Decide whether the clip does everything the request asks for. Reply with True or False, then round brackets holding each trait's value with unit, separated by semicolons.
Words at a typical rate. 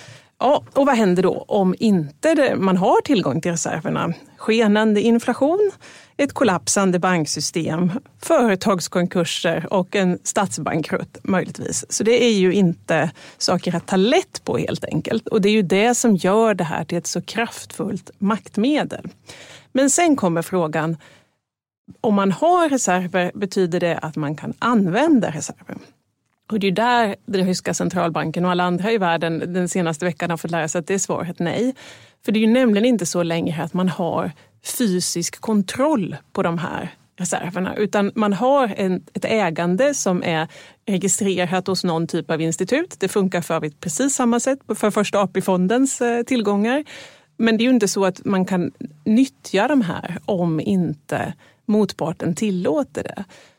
True (160 wpm)